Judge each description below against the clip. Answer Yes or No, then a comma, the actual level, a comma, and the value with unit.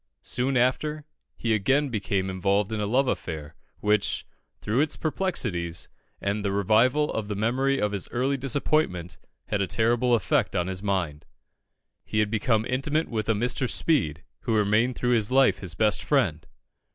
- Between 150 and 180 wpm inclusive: Yes, average, 165 wpm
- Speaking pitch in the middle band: No, low, 110 Hz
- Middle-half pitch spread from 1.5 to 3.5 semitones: No, average, 4.8 semitones